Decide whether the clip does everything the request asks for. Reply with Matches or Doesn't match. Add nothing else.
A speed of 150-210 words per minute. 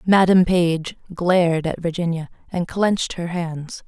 Doesn't match